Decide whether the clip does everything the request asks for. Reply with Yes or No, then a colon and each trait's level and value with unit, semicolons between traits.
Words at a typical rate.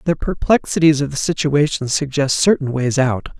Yes: average, 160 wpm